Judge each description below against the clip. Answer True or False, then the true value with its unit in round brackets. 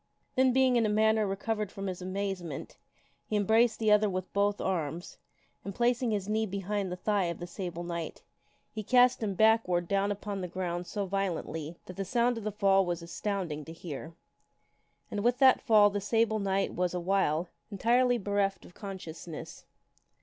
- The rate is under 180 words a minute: False (185 wpm)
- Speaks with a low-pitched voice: False (200 Hz)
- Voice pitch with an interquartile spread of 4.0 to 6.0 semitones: False (3.3 semitones)